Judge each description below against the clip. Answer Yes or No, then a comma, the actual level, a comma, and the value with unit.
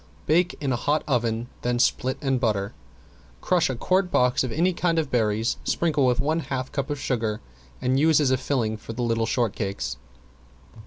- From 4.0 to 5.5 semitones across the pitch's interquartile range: Yes, average, 4.7 semitones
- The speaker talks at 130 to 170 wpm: No, average, 195 wpm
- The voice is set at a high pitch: No, low, 130 Hz